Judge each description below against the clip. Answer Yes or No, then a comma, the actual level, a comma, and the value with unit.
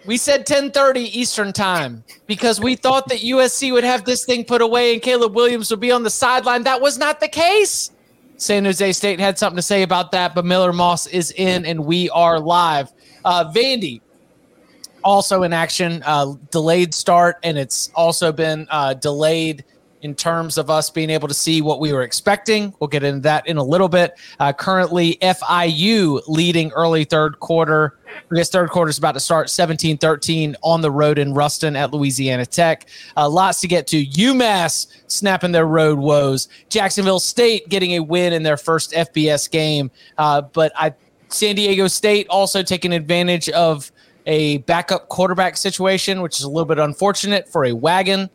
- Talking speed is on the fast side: No, average, 185 wpm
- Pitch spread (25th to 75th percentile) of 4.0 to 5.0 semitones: Yes, average, 4.3 semitones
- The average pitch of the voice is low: No, medium, 175 Hz